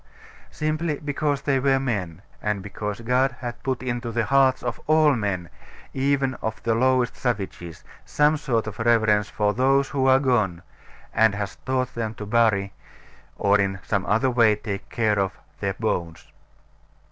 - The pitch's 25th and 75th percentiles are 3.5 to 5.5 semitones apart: Yes, average, 4.3 semitones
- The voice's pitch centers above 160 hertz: No, low, 115 Hz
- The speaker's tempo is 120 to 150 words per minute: No, average, 160 wpm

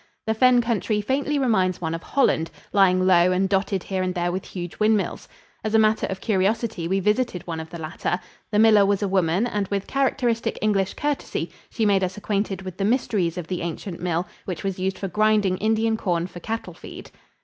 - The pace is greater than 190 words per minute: Yes, fast, 205 wpm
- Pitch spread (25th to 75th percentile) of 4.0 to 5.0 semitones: No, average, 3.2 semitones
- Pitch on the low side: No, high, 195 Hz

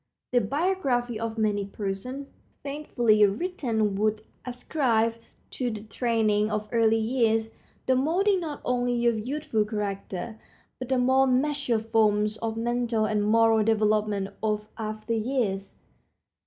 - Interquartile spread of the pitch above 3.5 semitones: No, average, 2.9 semitones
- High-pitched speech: Yes, high, 225 Hz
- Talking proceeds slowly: Yes, slow, 130 wpm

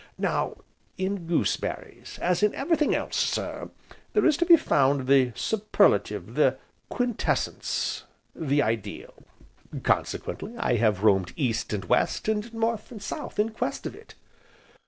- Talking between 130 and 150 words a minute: Yes, average, 140 wpm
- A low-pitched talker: No, medium, 180 Hz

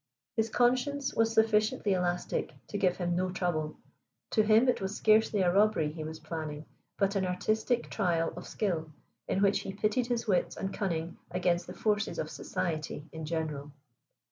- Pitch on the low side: No, high, 190 Hz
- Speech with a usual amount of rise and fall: Yes, average, 4.7 semitones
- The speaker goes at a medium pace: Yes, average, 170 wpm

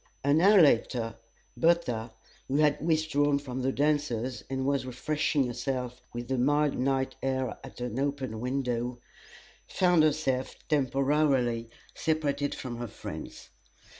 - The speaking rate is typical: No, slow, 130 wpm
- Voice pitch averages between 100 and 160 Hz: Yes, low, 135 Hz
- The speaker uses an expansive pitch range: No, average, 3.0 semitones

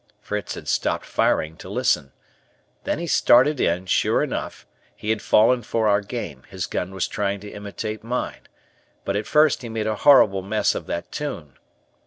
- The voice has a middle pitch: No, low, 105 Hz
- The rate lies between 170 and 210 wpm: Yes, average, 180 wpm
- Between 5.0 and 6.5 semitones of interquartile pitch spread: No, average, 3.7 semitones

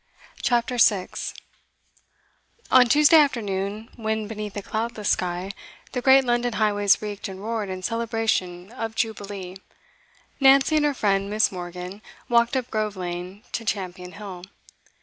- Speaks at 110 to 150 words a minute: Yes, slow, 135 wpm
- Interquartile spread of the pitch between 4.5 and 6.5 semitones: No, average, 3.5 semitones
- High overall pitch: Yes, high, 215 Hz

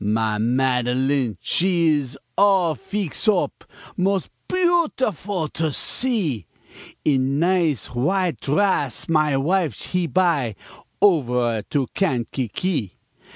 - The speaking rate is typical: No, slow, 100 wpm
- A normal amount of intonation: No, wide, 6.8 semitones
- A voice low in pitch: No, medium, 155 Hz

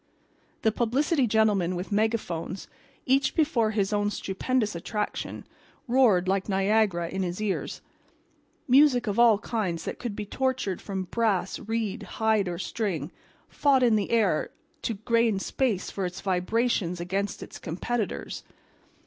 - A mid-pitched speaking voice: No, high, 210 Hz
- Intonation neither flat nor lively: Yes, average, 3.6 semitones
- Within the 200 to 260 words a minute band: No, average, 140 wpm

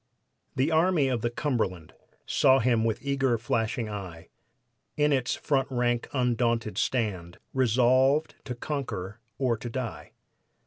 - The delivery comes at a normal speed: No, slow, 130 wpm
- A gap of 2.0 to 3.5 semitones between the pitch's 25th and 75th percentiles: Yes, average, 3.1 semitones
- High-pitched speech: No, low, 120 Hz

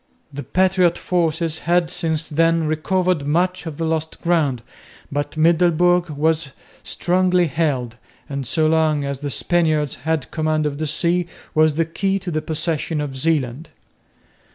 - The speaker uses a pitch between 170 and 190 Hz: No, medium, 160 Hz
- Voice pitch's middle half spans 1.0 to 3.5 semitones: Yes, narrow, 2.5 semitones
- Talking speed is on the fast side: No, average, 150 wpm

